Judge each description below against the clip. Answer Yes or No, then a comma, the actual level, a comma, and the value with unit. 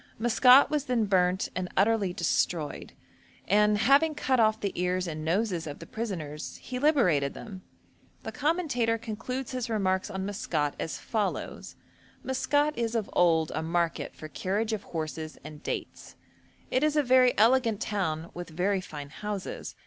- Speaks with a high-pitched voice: Yes, high, 205 Hz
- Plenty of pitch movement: Yes, wide, 5.9 semitones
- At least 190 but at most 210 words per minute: No, average, 155 wpm